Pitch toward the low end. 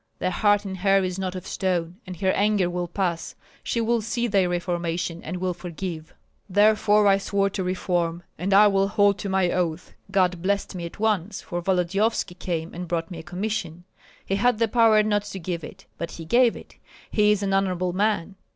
No: high, 190 Hz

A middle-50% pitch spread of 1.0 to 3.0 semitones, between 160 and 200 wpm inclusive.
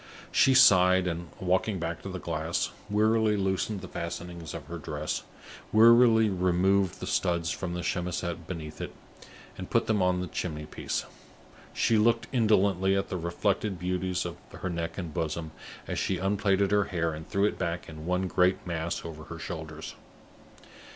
Yes: average, 2.7 semitones; average, 170 wpm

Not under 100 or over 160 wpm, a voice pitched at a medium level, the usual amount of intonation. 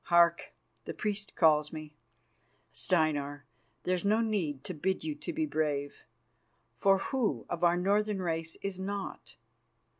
Yes: average, 140 wpm; medium, 180 Hz; average, 4.4 semitones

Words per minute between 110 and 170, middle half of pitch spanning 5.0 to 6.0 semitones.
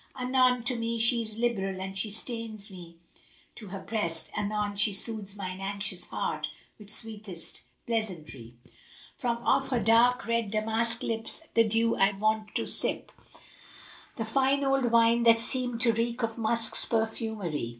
No: average, 160 wpm; narrow, 2.5 semitones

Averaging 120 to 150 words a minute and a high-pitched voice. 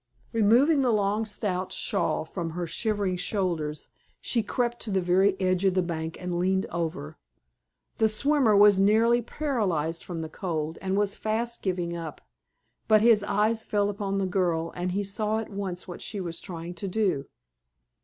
No: average, 175 wpm; high, 195 Hz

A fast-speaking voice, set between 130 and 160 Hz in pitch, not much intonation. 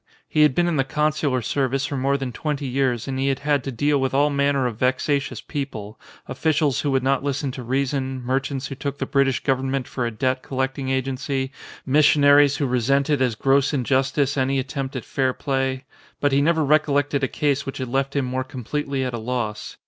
Yes: fast, 215 wpm; low, 135 Hz; narrow, 1.5 semitones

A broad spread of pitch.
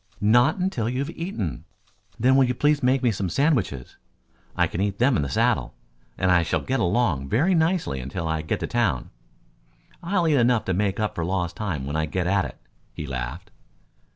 Yes: wide, 8.0 semitones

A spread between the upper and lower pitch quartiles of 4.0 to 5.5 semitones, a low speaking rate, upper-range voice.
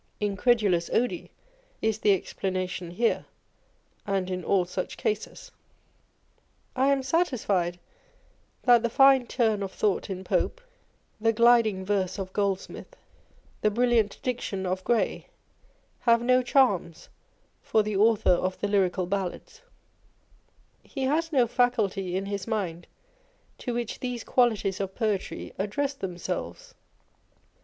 Yes: average, 4.3 semitones; slow, 125 wpm; high, 210 Hz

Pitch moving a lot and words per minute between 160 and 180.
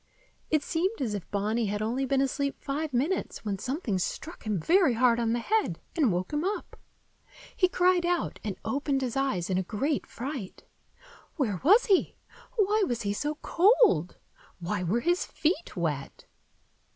Yes: wide, 8.2 semitones; average, 170 wpm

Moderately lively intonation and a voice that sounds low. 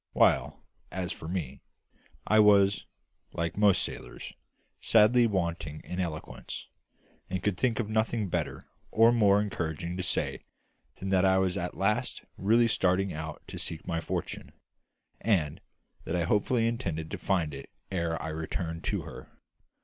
Yes: average, 4.3 semitones; very low, 95 Hz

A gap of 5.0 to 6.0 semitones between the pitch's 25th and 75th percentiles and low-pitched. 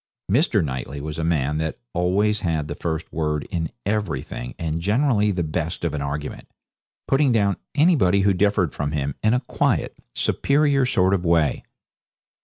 Yes: wide, 5.4 semitones; very low, 85 Hz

